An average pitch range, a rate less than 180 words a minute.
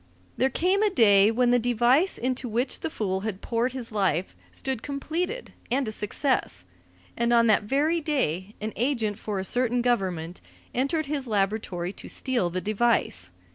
Yes: average, 4.6 semitones; average, 170 wpm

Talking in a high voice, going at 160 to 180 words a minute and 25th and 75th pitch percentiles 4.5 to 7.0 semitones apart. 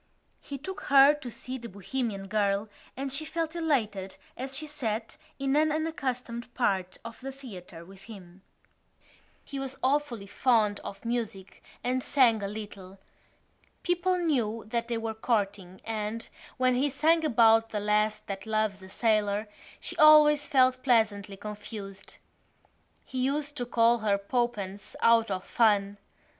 No: high, 230 Hz; average, 150 wpm; average, 4.8 semitones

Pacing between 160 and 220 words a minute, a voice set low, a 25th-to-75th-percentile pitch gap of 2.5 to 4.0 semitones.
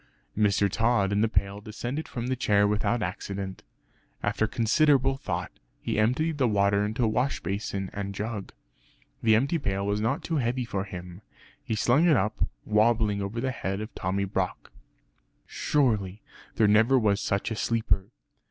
Yes: average, 165 wpm; low, 110 Hz; average, 3.3 semitones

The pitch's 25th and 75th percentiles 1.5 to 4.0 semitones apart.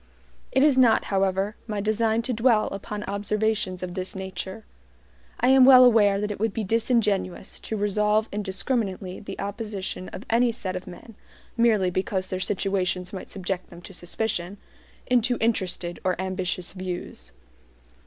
Yes: average, 3.1 semitones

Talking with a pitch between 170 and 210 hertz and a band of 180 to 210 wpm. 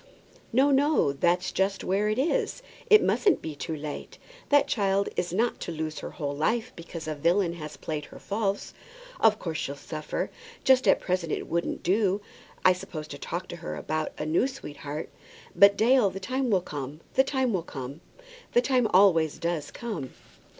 Yes: medium, 185 Hz; average, 185 wpm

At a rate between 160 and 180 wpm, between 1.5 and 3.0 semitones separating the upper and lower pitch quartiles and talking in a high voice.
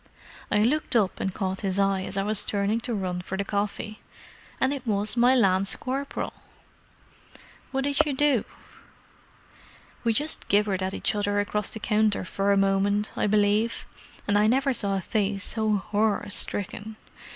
Yes: average, 165 wpm; narrow, 2.5 semitones; high, 205 Hz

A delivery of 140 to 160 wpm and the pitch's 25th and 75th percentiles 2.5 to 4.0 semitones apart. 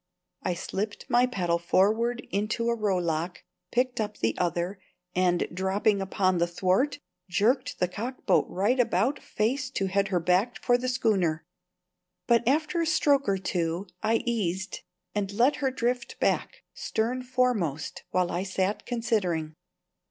No: average, 145 wpm; average, 5.0 semitones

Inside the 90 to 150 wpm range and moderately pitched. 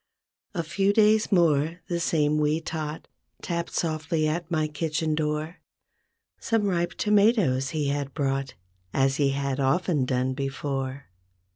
Yes: slow, 135 wpm; medium, 155 Hz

